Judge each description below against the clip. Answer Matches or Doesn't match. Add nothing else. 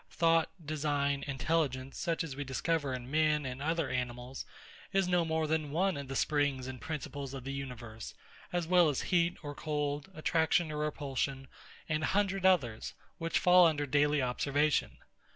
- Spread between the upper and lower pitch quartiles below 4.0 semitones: Matches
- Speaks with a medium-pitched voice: Matches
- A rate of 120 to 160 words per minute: Doesn't match